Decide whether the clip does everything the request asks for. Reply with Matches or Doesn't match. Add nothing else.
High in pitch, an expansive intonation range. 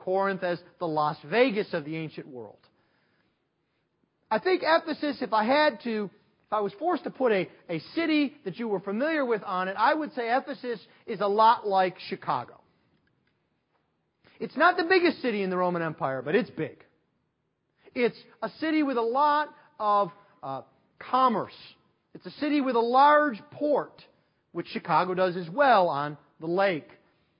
Matches